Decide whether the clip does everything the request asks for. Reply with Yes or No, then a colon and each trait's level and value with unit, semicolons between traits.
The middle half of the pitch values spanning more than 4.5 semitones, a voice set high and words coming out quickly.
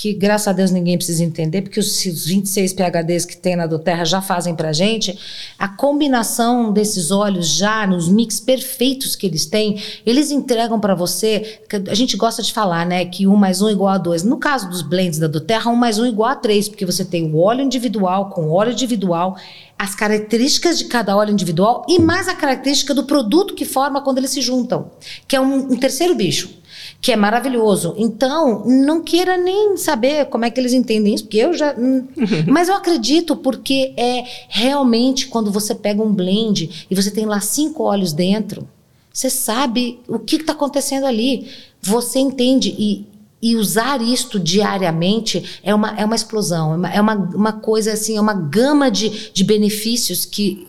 Yes: average, 5.1 semitones; high, 215 Hz; fast, 195 wpm